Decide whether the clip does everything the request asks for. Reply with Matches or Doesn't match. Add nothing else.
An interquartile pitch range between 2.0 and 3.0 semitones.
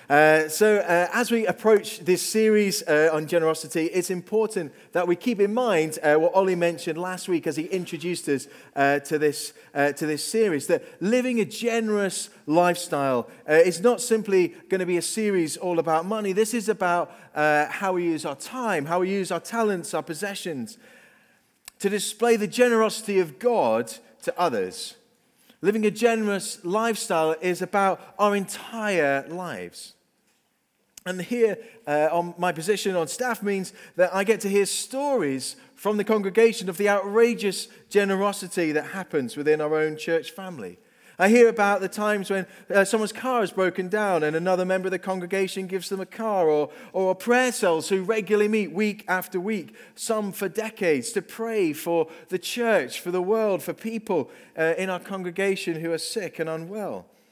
Doesn't match